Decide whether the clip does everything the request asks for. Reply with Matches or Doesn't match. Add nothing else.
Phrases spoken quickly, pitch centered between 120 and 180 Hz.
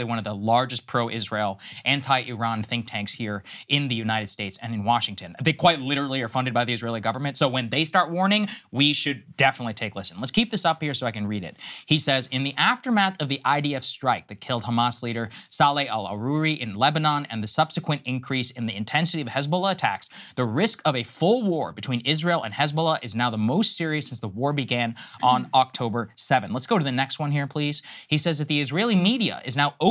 Matches